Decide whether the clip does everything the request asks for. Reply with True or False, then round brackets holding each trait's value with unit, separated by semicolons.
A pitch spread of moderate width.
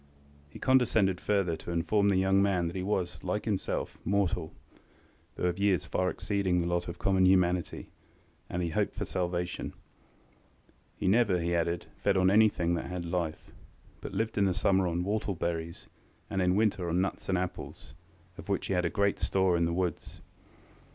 False (2.2 semitones)